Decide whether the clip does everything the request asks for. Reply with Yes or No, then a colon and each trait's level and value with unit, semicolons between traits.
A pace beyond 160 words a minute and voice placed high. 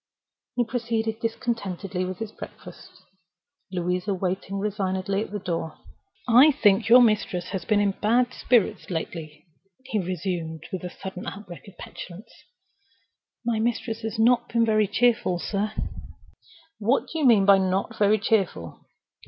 No: average, 145 wpm; high, 205 Hz